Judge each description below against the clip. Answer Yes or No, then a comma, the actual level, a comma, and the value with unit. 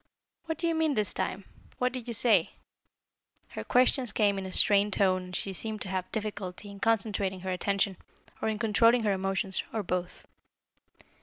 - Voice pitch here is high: Yes, high, 205 Hz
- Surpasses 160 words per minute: Yes, average, 180 wpm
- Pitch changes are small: No, average, 3.1 semitones